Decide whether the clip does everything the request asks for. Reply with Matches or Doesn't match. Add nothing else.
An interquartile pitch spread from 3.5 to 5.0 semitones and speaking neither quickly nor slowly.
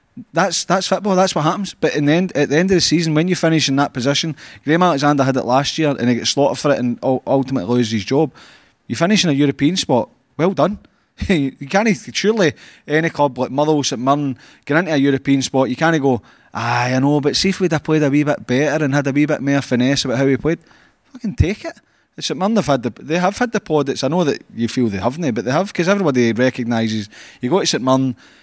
Doesn't match